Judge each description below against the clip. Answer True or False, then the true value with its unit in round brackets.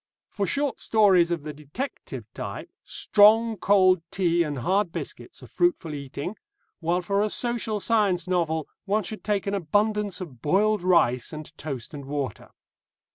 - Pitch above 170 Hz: True (185 Hz)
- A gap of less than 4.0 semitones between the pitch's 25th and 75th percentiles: False (5.2 semitones)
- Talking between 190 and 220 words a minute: False (155 wpm)